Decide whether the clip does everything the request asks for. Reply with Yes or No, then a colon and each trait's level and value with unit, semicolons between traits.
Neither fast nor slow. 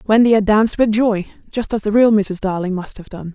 No: fast, 250 wpm